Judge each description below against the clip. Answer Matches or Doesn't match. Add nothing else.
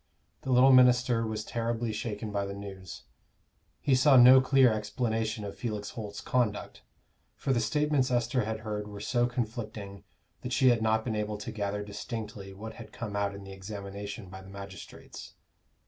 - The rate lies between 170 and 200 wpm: Matches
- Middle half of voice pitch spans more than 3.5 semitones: Doesn't match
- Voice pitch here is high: Doesn't match